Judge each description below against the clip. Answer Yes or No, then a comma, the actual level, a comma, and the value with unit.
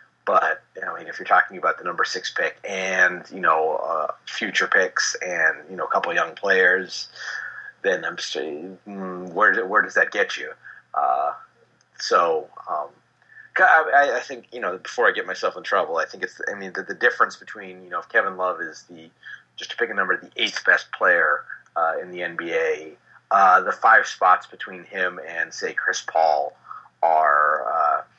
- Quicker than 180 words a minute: Yes, average, 195 wpm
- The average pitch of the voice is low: Yes, low, 100 Hz